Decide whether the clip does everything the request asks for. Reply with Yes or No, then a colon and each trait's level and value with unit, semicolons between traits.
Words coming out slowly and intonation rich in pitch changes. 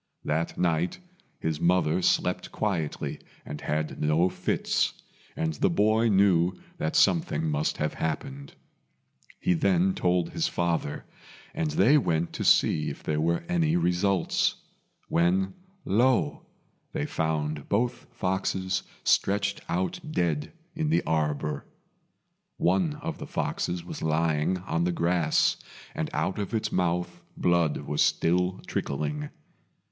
No: slow, 130 wpm; average, 3.7 semitones